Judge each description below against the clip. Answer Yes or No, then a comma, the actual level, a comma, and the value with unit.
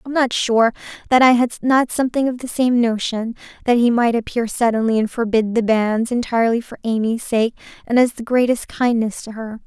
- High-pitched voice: Yes, high, 235 Hz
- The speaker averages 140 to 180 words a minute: No, average, 200 wpm